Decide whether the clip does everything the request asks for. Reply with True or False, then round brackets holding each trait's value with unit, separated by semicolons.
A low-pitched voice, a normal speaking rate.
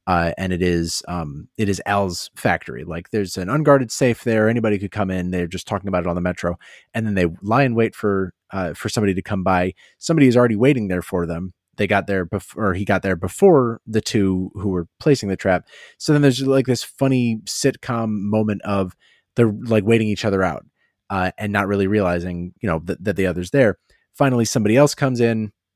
False (100 Hz; 220 wpm)